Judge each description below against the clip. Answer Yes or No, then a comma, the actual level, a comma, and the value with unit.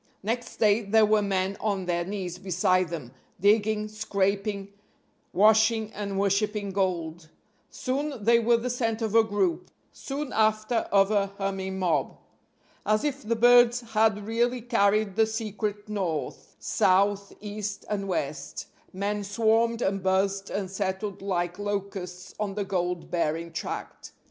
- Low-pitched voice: No, high, 205 Hz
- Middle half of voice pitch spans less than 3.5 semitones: Yes, narrow, 2.5 semitones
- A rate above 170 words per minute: No, average, 140 wpm